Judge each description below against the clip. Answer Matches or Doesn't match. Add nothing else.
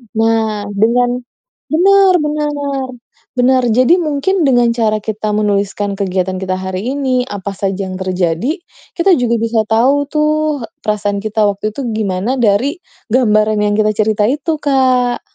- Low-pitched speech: Doesn't match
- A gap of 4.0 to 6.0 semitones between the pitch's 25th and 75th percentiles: Matches